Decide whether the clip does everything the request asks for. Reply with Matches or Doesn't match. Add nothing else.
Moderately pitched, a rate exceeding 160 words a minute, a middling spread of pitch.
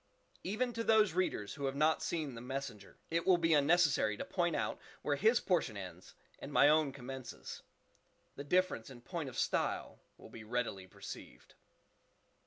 Doesn't match